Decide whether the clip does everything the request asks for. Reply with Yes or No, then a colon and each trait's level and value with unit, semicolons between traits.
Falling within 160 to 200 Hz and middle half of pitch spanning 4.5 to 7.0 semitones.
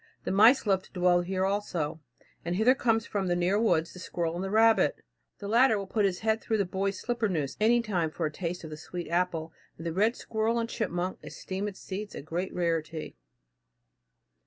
No: high, 190 Hz; average, 4.0 semitones